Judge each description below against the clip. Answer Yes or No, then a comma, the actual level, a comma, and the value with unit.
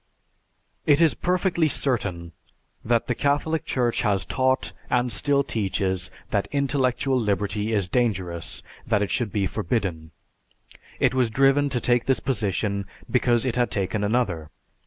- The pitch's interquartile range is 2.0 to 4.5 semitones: No, average, 4.9 semitones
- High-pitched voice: No, low, 120 Hz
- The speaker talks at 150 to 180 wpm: No, average, 140 wpm